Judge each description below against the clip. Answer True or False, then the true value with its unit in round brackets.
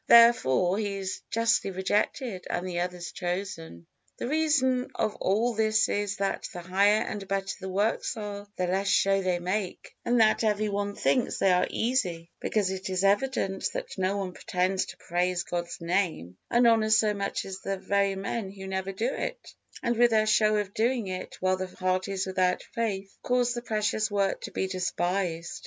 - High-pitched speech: True (195 Hz)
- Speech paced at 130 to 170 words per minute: False (185 wpm)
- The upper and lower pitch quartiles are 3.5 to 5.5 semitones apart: False (2.8 semitones)